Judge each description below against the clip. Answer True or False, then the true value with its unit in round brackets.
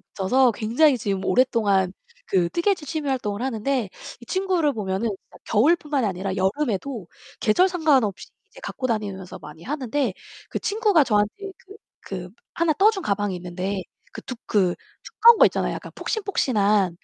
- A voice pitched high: True (230 Hz)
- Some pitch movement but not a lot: False (7.4 semitones)